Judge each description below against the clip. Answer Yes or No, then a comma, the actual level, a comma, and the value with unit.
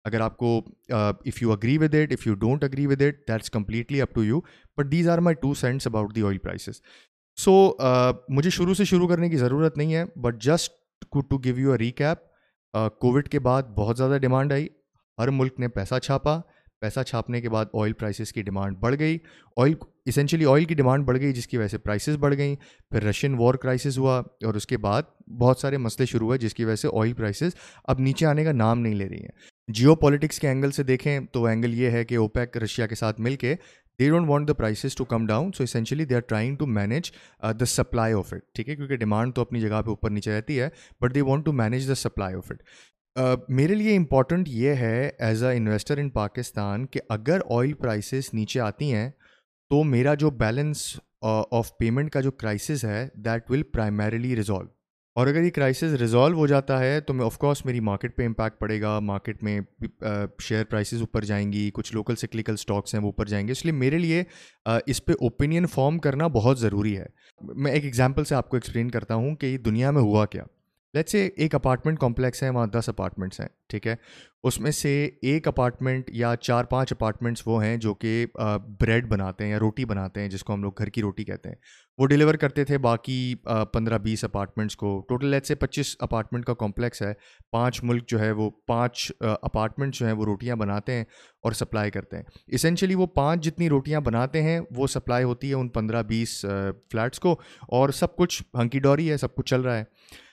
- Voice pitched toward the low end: Yes, low, 125 Hz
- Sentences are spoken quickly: Yes, fast, 215 wpm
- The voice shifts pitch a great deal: No, average, 4.3 semitones